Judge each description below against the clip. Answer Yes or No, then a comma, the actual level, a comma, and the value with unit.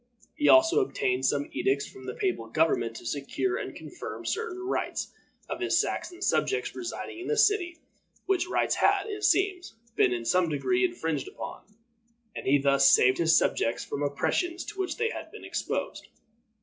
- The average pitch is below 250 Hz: No, very high, 325 Hz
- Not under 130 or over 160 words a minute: No, average, 175 wpm